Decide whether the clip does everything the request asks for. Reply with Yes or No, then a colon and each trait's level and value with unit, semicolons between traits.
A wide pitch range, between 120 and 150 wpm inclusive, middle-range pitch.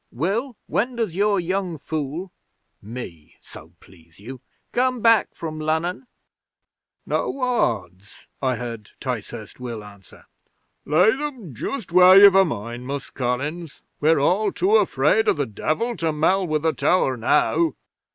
Yes: wide, 8.5 semitones; average, 140 wpm; medium, 160 Hz